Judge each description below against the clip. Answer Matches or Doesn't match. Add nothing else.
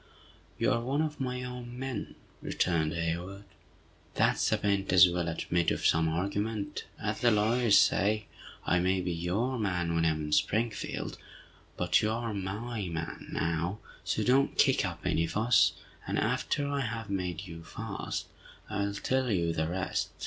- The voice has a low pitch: Matches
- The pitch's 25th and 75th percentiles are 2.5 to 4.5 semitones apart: Doesn't match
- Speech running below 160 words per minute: Doesn't match